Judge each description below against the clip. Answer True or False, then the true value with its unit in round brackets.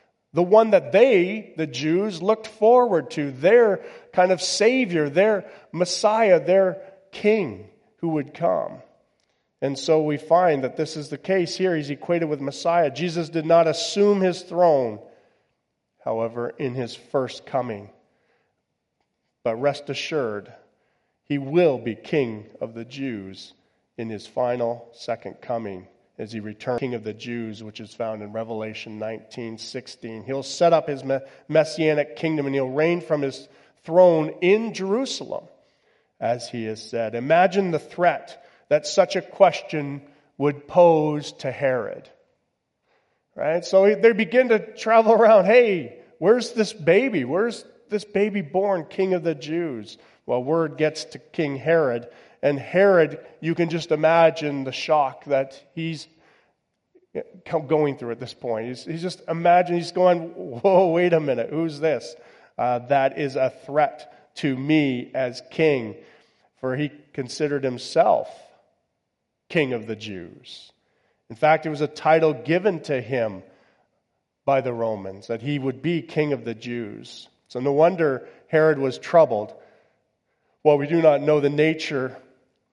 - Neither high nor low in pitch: True (155 Hz)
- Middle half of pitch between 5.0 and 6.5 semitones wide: True (5.3 semitones)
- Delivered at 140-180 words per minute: True (150 wpm)